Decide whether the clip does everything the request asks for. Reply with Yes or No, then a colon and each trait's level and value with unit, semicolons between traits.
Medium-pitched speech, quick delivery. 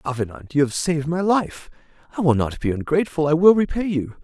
Yes: medium, 150 Hz; fast, 210 wpm